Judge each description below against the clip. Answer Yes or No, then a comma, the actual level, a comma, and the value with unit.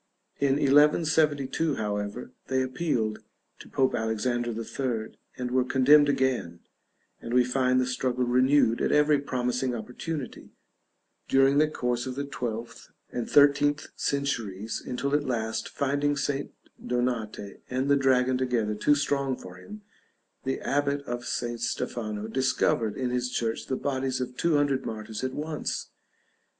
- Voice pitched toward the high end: No, low, 130 Hz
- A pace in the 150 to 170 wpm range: No, average, 140 wpm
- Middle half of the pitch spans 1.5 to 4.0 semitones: Yes, average, 2.9 semitones